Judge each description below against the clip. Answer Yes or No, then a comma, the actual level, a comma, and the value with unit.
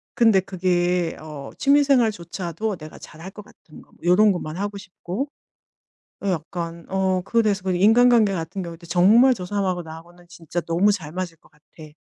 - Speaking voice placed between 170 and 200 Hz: Yes, medium, 185 Hz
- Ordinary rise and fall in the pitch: Yes, average, 3.3 semitones